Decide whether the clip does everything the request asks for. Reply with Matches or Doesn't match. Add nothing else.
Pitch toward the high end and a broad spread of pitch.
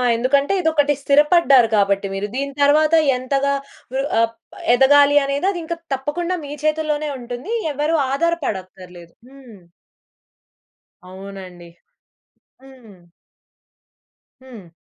Matches